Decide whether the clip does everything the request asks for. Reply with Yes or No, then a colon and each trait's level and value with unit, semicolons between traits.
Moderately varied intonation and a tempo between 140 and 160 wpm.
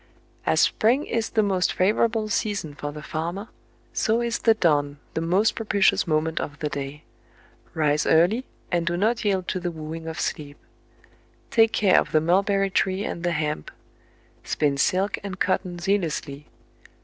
No: average, 4.8 semitones; average, 175 wpm